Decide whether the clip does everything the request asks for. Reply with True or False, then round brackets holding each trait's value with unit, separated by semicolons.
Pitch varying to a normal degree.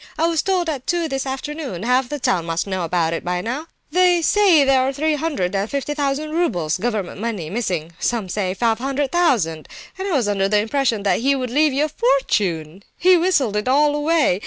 False (7.4 semitones)